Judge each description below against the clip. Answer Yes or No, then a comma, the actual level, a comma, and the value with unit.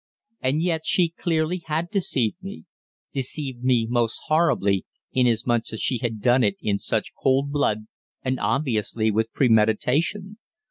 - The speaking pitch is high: No, low, 130 Hz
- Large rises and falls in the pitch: Yes, wide, 5.9 semitones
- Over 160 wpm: No, average, 140 wpm